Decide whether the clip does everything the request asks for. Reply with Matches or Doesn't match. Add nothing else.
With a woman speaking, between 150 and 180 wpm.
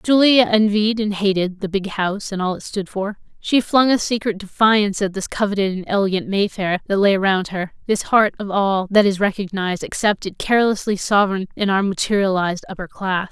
Doesn't match